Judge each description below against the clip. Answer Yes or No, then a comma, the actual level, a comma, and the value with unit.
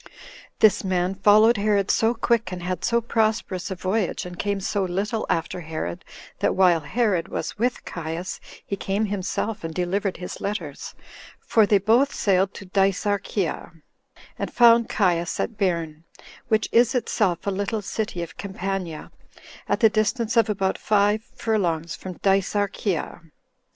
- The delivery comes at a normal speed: Yes, average, 150 wpm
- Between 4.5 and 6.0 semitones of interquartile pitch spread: No, average, 3.1 semitones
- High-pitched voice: Yes, high, 195 Hz